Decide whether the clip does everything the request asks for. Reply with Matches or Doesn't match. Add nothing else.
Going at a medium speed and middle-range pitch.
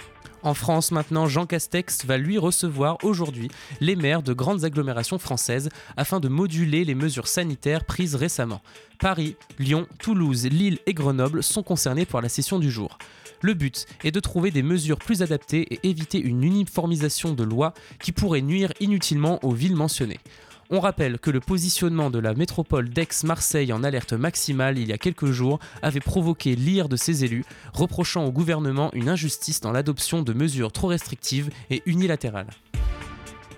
Matches